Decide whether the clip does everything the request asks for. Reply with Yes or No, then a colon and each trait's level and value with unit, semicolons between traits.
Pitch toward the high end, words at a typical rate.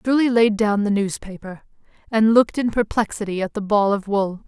Yes: high, 210 Hz; average, 190 wpm